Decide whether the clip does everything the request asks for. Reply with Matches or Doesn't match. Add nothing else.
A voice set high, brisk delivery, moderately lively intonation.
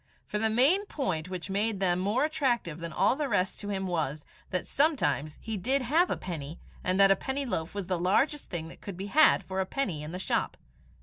Doesn't match